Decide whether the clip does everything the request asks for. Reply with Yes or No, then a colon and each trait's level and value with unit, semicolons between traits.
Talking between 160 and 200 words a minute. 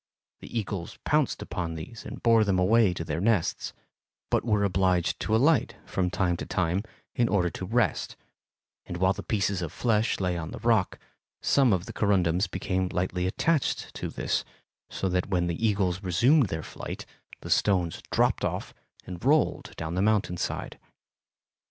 Yes: average, 170 wpm